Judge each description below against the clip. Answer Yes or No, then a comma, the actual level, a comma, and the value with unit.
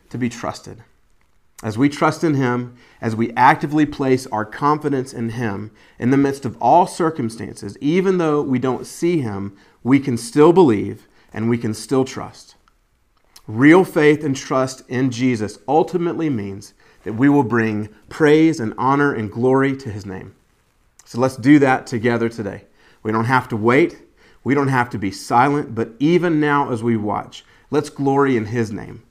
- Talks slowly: No, average, 175 wpm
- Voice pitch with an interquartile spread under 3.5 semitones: No, average, 4.2 semitones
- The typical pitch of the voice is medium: No, low, 130 Hz